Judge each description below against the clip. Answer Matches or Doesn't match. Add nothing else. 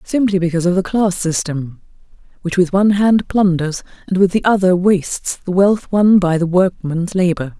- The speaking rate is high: Doesn't match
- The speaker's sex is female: Matches